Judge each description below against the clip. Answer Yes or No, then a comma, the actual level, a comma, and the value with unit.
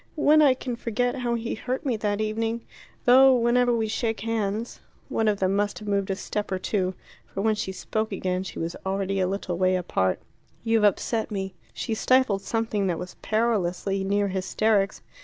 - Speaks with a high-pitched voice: Yes, high, 210 Hz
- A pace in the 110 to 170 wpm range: No, average, 195 wpm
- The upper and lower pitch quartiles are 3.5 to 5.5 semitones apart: No, average, 3.1 semitones